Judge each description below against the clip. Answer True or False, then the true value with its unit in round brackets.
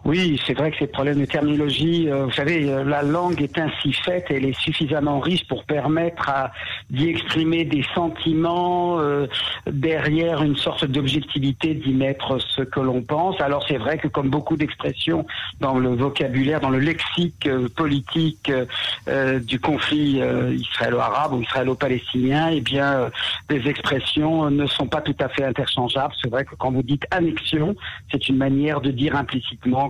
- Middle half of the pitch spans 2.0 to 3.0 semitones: True (2.7 semitones)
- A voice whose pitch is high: False (145 Hz)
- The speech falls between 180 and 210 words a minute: False (170 wpm)